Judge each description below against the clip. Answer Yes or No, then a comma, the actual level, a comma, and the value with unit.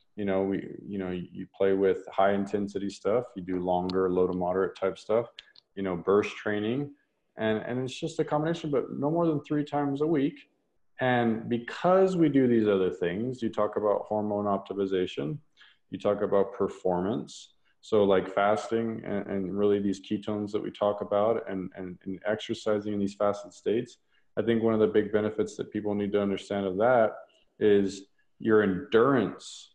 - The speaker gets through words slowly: No, average, 180 wpm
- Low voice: Yes, low, 105 Hz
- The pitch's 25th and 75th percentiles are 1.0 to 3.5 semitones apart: Yes, average, 2.9 semitones